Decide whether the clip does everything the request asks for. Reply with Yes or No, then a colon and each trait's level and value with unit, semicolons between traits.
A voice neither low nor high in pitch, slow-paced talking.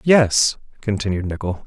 No: low, 105 Hz; slow, 110 wpm